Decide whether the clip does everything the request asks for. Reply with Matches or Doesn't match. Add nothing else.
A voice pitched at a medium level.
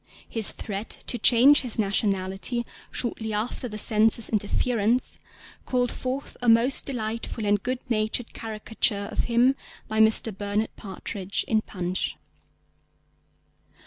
Doesn't match